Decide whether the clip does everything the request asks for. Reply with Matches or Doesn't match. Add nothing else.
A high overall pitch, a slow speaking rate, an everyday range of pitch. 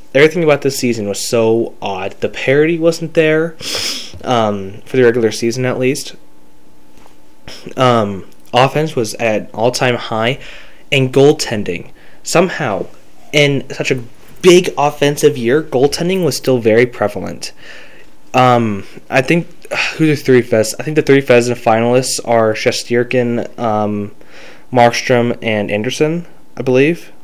Doesn't match